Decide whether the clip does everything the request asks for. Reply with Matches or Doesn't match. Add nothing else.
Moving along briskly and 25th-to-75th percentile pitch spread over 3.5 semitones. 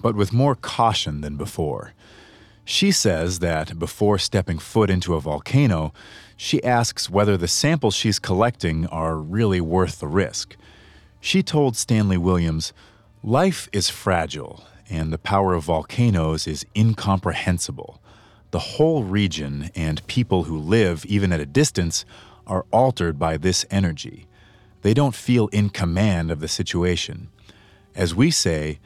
Doesn't match